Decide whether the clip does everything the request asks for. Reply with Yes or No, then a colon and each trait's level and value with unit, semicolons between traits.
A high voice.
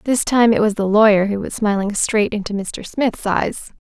Yes: high, 210 Hz